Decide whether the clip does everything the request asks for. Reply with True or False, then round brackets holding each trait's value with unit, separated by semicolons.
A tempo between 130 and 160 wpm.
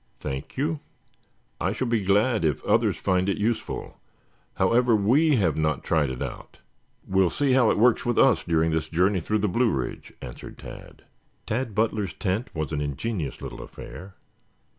False (170 wpm)